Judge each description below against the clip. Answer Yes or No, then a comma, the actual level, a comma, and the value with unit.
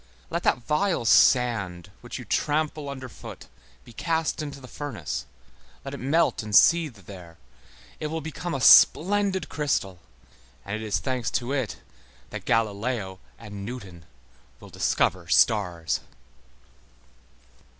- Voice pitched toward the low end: Yes, low, 125 Hz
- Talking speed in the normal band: No, slow, 130 wpm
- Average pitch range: No, wide, 7.0 semitones